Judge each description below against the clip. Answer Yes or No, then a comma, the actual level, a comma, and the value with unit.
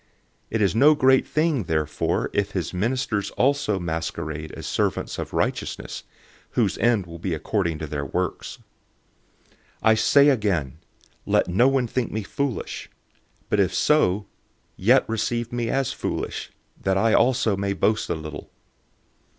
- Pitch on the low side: Yes, low, 105 Hz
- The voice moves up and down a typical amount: No, wide, 6.5 semitones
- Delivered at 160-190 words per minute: No, average, 150 wpm